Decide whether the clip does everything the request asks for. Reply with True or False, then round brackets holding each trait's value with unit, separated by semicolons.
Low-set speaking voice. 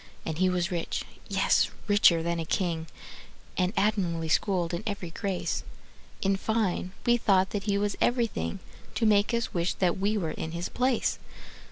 False (190 Hz)